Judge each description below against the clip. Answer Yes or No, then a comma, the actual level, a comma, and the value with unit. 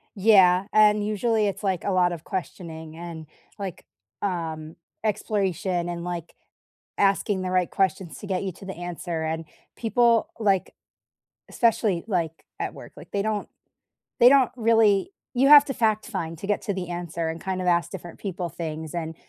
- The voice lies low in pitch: No, medium, 185 Hz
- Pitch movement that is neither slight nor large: Yes, average, 3.5 semitones